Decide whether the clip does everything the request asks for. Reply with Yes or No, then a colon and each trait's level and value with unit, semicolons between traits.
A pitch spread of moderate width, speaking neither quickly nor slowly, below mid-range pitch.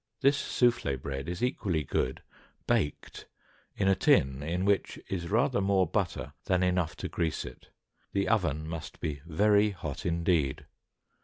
Yes: average, 4.5 semitones; average, 150 wpm; very low, 90 Hz